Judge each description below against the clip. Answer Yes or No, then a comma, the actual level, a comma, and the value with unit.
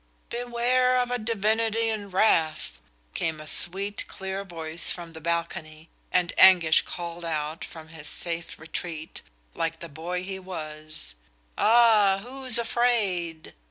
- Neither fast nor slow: No, slow, 130 wpm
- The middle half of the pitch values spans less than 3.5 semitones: No, average, 5.3 semitones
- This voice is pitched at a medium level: Yes, medium, 180 Hz